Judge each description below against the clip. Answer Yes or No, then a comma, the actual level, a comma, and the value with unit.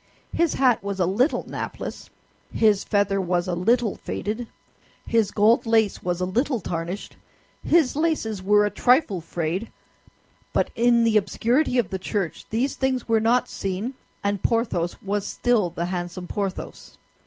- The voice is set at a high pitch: Yes, high, 210 Hz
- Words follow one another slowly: No, average, 155 wpm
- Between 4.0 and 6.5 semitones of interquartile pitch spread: Yes, average, 4.3 semitones